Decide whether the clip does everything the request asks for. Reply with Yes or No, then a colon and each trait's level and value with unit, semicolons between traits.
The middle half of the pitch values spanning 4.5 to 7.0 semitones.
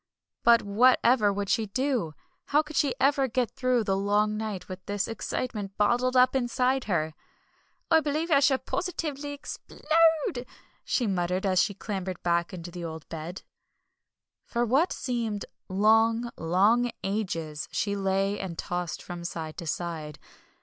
Yes: wide, 5.5 semitones